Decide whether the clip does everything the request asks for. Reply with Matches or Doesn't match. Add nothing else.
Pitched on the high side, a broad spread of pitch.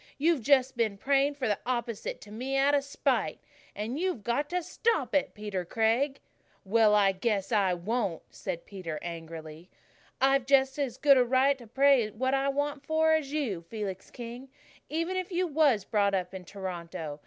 Matches